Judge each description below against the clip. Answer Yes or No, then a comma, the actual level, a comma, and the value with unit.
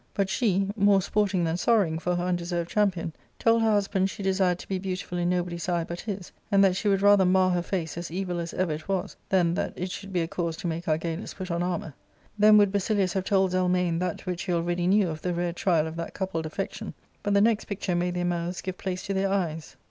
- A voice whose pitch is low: No, medium, 180 Hz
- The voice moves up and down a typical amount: No, narrow, 2.2 semitones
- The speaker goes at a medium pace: No, fast, 245 wpm